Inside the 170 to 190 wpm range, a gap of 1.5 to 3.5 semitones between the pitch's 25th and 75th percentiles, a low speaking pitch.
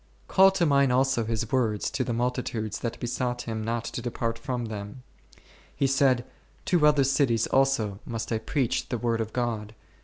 Yes: average, 185 wpm; average, 2.8 semitones; low, 120 Hz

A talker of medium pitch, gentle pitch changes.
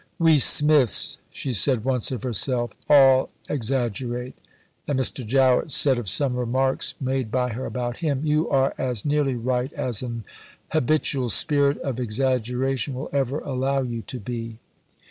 No: low, 130 Hz; narrow, 2.2 semitones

